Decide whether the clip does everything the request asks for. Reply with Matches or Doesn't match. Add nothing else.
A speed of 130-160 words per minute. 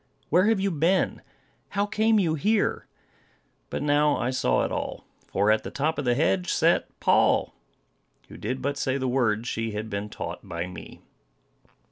Doesn't match